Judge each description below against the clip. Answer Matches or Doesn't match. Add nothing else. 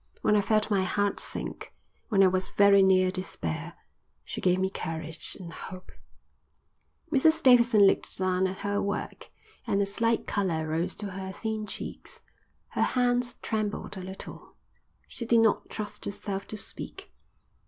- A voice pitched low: Doesn't match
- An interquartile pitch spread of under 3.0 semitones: Matches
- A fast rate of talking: Doesn't match